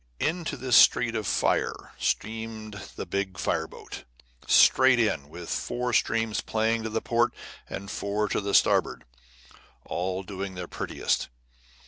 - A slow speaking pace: Yes, slow, 130 wpm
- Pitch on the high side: No, low, 110 Hz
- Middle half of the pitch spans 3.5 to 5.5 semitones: No, average, 2.9 semitones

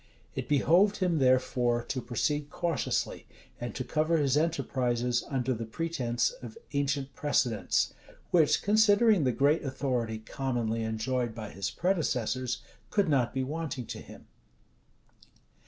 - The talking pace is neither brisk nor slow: No, slow, 130 wpm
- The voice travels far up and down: No, average, 4.4 semitones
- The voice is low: Yes, low, 130 Hz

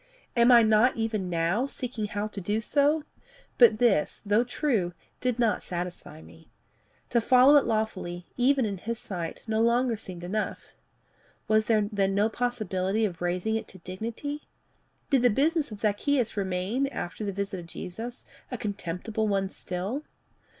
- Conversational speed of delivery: Yes, average, 160 wpm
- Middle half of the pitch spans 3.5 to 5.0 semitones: Yes, average, 4.3 semitones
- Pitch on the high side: Yes, high, 215 Hz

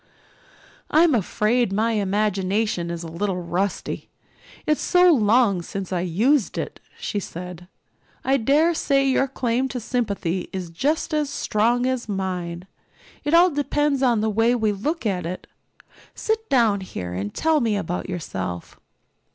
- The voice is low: No, high, 215 Hz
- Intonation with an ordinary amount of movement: No, wide, 6.7 semitones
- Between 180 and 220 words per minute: No, average, 150 wpm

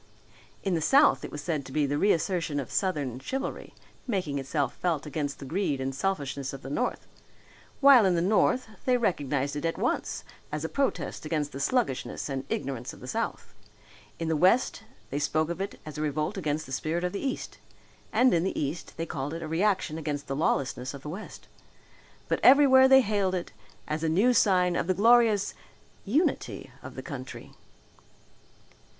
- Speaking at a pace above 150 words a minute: Yes, average, 190 wpm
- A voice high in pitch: No, medium, 165 Hz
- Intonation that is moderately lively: No, wide, 5.7 semitones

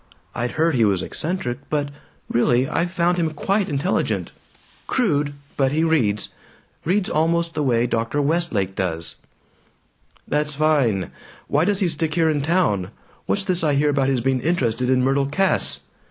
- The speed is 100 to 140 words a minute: No, average, 160 wpm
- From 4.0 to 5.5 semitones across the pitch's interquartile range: Yes, average, 5.1 semitones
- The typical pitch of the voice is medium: Yes, medium, 145 Hz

